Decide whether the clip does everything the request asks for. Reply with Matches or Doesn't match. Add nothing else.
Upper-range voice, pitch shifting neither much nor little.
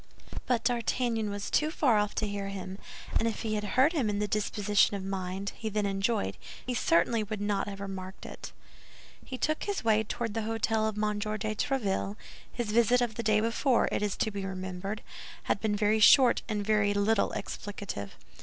Doesn't match